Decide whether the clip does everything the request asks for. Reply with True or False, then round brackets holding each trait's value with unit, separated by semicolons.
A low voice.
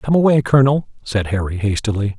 True (120 Hz)